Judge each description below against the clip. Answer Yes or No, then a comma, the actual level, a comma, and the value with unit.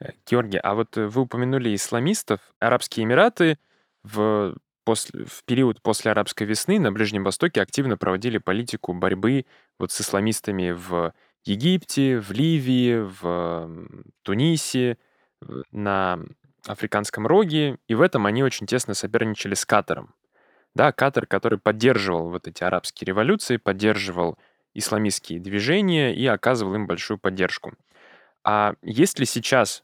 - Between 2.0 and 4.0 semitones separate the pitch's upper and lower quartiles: No, average, 4.5 semitones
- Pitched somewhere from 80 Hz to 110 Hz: Yes, low, 105 Hz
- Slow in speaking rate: No, average, 125 wpm